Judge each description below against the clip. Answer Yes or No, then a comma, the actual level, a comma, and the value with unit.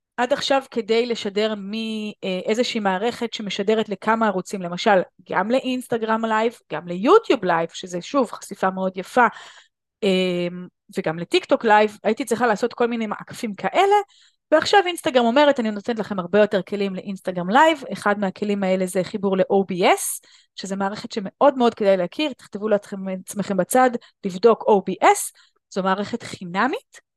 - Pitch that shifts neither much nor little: Yes, average, 4.0 semitones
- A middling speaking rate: Yes, average, 140 wpm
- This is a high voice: Yes, high, 210 Hz